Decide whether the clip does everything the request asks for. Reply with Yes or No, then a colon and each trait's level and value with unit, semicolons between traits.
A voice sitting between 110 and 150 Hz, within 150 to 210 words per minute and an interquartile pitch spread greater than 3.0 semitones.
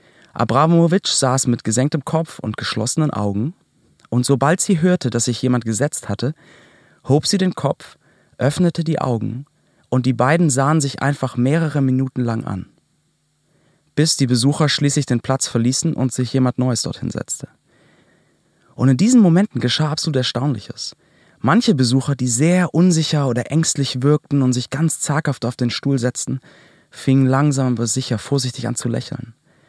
Yes: low, 135 Hz; average, 160 wpm; average, 4.1 semitones